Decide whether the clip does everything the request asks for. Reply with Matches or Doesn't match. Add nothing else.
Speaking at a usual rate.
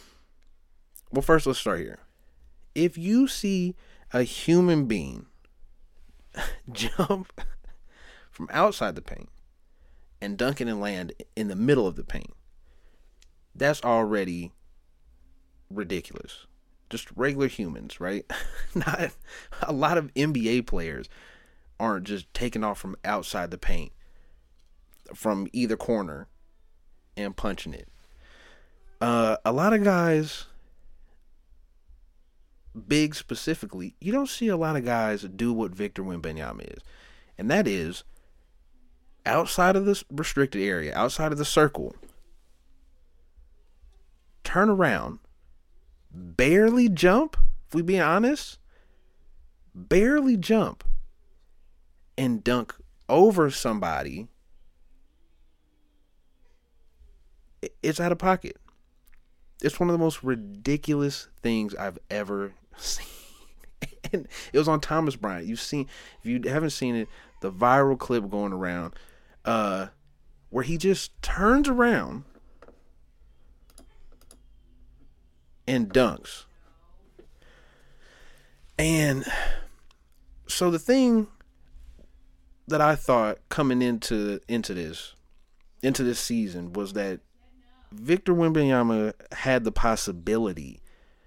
Doesn't match